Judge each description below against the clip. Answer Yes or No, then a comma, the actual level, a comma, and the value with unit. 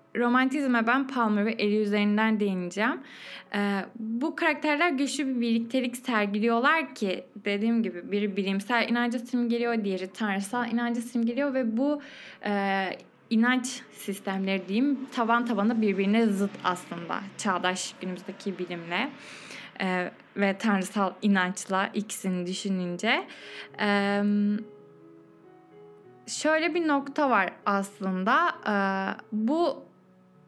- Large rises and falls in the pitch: No, average, 4.0 semitones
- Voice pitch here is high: Yes, high, 210 Hz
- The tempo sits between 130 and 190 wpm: No, average, 105 wpm